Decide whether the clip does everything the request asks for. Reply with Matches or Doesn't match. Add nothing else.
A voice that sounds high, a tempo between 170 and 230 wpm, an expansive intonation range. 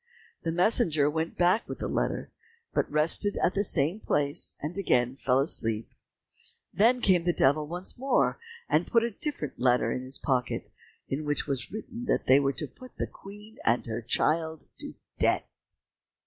Doesn't match